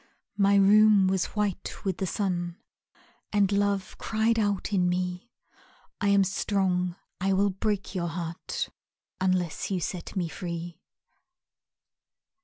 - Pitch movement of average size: No, narrow, 2.1 semitones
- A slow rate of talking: Yes, slow, 125 wpm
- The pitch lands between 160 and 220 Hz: Yes, high, 190 Hz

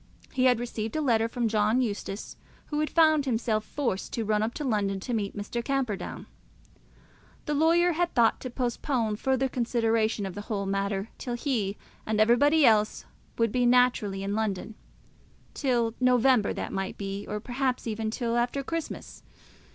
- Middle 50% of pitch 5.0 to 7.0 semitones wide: No, average, 3.4 semitones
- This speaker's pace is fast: No, average, 165 wpm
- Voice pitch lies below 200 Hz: No, high, 230 Hz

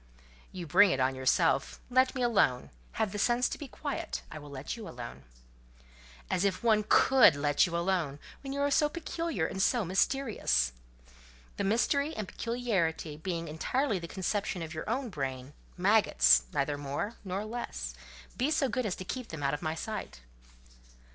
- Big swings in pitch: Yes, wide, 8.4 semitones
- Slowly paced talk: No, average, 170 wpm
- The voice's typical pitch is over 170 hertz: Yes, high, 190 Hz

